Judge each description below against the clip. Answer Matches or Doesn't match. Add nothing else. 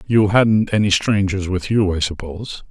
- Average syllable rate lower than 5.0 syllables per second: Matches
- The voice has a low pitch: Matches